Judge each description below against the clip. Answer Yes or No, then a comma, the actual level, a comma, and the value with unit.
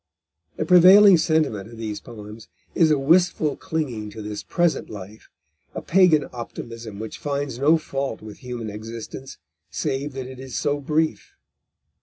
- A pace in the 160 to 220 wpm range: No, average, 150 wpm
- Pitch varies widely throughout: Yes, wide, 5.9 semitones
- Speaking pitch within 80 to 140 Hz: Yes, low, 135 Hz